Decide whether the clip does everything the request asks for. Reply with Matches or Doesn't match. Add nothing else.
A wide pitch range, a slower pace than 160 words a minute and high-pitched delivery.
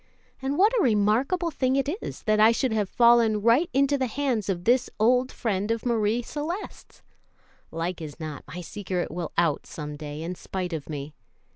Doesn't match